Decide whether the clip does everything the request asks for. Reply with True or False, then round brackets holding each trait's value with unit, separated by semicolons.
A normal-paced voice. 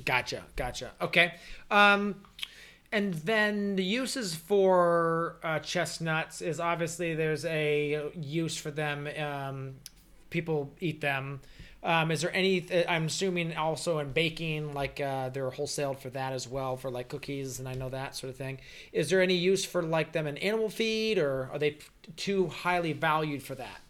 True (170 wpm)